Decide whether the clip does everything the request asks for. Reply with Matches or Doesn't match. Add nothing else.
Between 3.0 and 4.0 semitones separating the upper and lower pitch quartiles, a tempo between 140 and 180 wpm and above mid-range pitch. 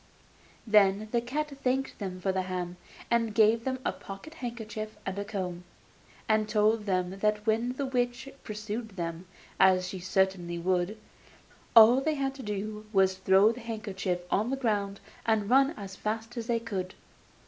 Matches